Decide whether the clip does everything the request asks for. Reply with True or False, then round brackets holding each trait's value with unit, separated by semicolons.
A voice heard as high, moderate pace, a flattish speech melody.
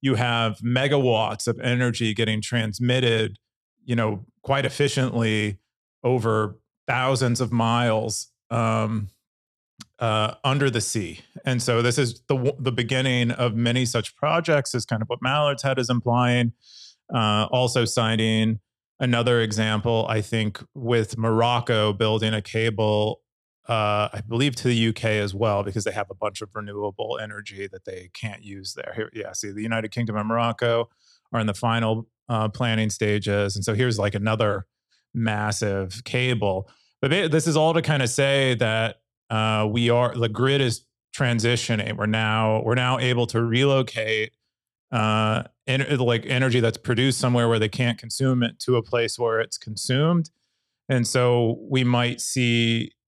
False (115 Hz; 160 wpm; 2.3 semitones)